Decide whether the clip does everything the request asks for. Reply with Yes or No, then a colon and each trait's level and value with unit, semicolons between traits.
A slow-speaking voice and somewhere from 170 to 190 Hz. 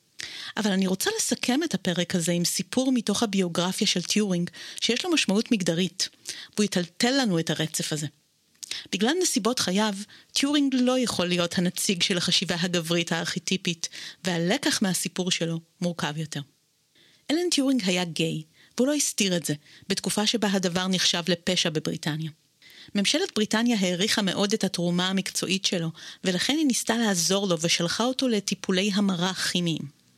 No: average, 145 wpm; medium, 185 Hz